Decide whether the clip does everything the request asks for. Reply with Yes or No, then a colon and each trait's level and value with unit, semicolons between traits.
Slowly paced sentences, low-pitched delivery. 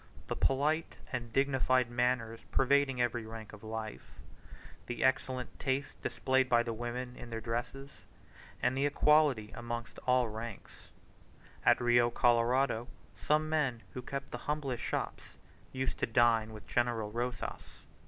No: average, 145 wpm; low, 120 Hz